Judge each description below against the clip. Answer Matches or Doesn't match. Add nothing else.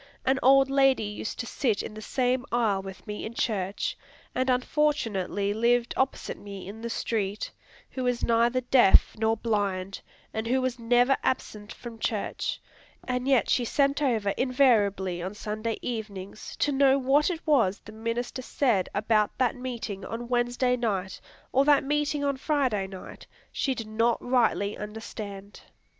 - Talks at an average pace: Matches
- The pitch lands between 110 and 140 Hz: Doesn't match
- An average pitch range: Matches